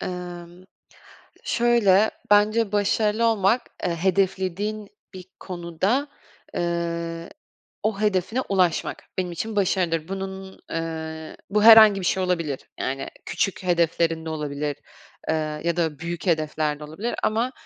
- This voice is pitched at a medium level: Yes, medium, 180 Hz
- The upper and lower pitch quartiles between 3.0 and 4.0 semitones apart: Yes, average, 3.6 semitones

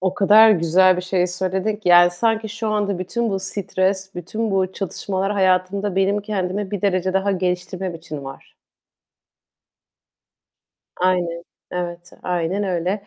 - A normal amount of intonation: No, narrow, 2.1 semitones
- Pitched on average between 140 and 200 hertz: Yes, high, 190 Hz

